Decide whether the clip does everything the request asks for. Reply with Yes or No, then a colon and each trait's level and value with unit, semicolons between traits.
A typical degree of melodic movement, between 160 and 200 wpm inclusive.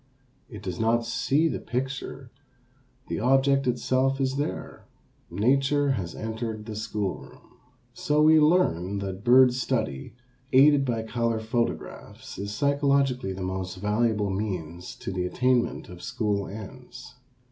No: average, 4.8 semitones; slow, 135 wpm